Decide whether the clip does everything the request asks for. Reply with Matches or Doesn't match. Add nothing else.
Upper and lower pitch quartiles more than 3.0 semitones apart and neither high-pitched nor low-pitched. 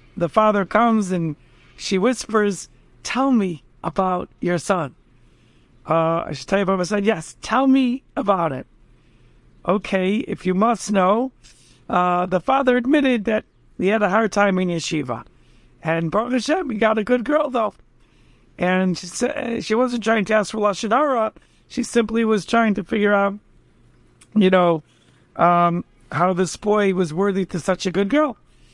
Doesn't match